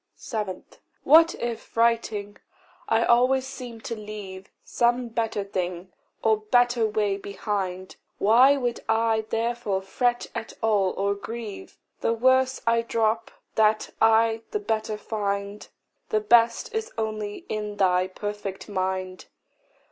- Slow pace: Yes, slow, 125 wpm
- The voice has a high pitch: Yes, high, 220 Hz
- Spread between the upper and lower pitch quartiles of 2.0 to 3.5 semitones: Yes, narrow, 2.6 semitones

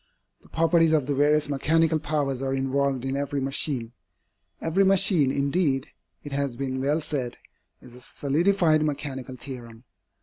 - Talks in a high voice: No, medium, 140 Hz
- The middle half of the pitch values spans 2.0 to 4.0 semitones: Yes, average, 2.8 semitones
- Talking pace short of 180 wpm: Yes, average, 145 wpm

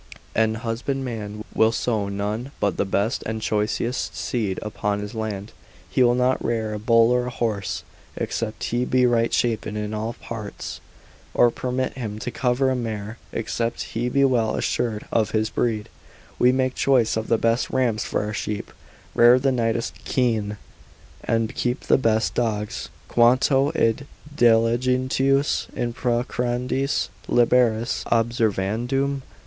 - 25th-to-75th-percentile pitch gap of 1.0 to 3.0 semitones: Yes, narrow, 2.4 semitones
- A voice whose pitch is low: Yes, low, 115 Hz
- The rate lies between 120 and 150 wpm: Yes, average, 145 wpm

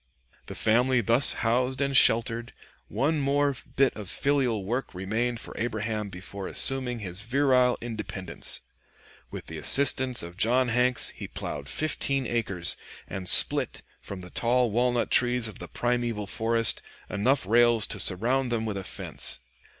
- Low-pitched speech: Yes, low, 120 Hz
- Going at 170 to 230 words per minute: No, average, 150 wpm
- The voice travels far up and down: No, average, 3.3 semitones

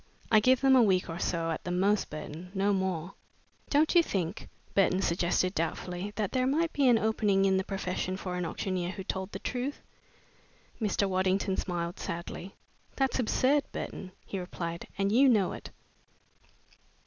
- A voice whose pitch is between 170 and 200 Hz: Yes, high, 190 Hz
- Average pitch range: Yes, average, 3.5 semitones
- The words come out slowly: No, average, 170 wpm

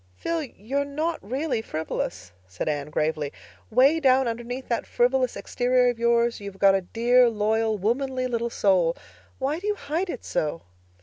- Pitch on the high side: Yes, high, 240 Hz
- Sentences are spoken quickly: No, average, 165 wpm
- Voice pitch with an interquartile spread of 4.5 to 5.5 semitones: Yes, average, 4.8 semitones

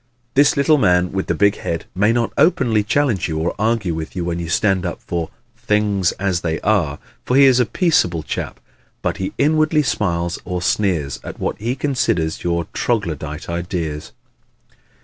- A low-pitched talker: Yes, very low, 95 Hz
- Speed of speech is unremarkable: Yes, average, 175 wpm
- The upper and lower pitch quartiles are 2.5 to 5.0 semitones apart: No, wide, 5.6 semitones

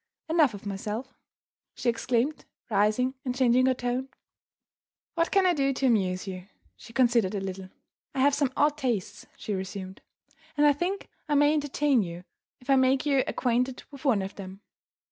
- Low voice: No, very high, 250 Hz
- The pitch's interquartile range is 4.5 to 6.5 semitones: Yes, wide, 5.4 semitones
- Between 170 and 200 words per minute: Yes, average, 175 wpm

